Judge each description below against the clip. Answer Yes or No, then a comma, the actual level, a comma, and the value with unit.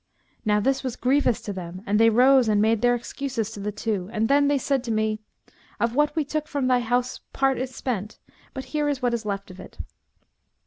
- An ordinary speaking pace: No, fast, 225 wpm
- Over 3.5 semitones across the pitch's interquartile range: Yes, average, 4.0 semitones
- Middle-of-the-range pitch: No, high, 240 Hz